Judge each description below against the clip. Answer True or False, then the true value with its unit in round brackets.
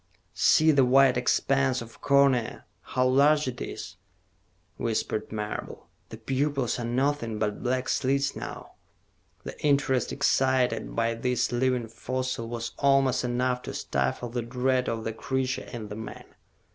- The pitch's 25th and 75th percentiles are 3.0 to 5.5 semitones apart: False (2.5 semitones)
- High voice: False (125 Hz)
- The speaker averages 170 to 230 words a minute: False (145 wpm)